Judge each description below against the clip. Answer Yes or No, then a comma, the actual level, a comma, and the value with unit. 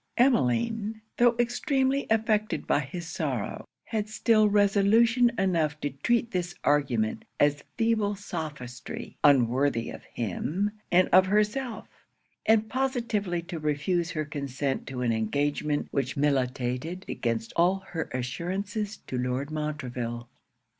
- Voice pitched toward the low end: No, medium, 170 Hz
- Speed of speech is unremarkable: No, slow, 120 wpm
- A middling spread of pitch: No, wide, 7.6 semitones